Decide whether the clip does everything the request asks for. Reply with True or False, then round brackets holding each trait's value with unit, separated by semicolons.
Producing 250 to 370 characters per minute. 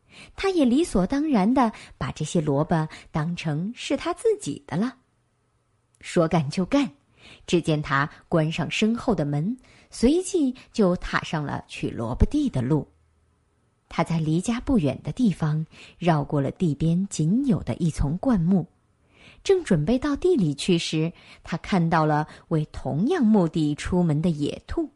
False (210 characters per minute)